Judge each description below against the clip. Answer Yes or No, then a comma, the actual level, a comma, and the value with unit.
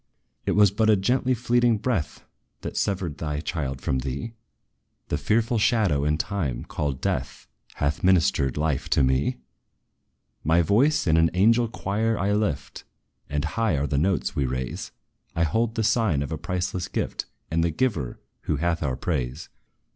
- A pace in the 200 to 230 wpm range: No, average, 165 wpm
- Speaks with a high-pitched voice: No, very low, 85 Hz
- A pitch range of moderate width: No, wide, 7.1 semitones